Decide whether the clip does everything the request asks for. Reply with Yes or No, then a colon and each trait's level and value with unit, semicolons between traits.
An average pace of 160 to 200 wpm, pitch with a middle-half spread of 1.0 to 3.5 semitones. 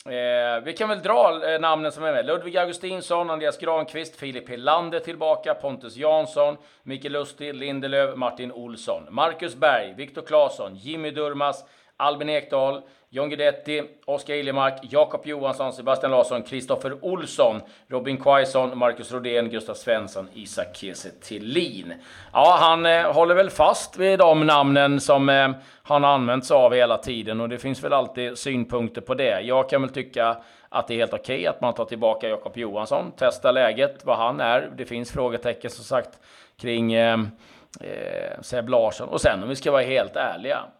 No: average, 170 wpm; average, 4.1 semitones